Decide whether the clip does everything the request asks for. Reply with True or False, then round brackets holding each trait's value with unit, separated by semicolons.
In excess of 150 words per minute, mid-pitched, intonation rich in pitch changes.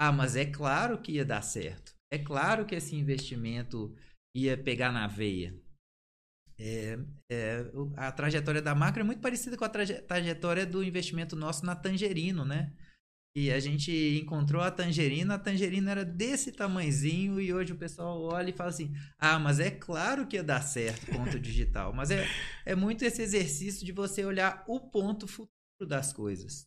True (180 wpm; 155 Hz; 6.0 semitones)